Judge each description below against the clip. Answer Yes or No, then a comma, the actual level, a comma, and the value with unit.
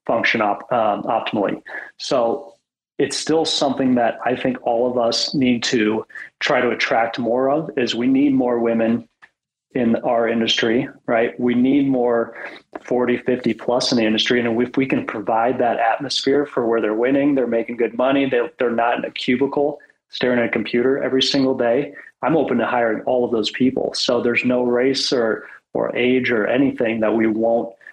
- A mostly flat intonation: Yes, narrow, 2.2 semitones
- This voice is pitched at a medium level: No, low, 125 Hz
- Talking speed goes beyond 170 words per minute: Yes, average, 190 wpm